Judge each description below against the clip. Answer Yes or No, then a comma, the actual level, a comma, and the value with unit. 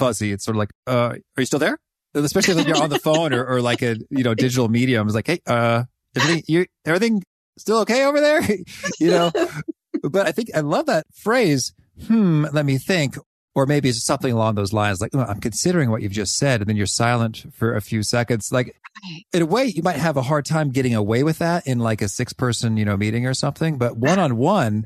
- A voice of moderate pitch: No, low, 130 Hz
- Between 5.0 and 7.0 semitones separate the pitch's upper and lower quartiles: Yes, wide, 5.6 semitones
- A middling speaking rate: No, fast, 240 wpm